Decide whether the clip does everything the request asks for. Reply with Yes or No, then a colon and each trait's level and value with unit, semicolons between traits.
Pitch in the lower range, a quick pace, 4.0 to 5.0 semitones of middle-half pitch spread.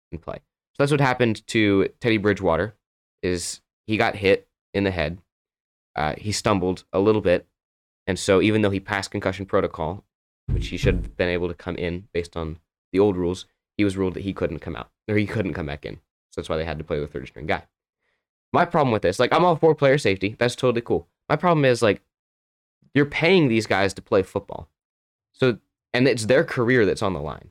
Yes: low, 100 Hz; fast, 225 wpm; average, 4.5 semitones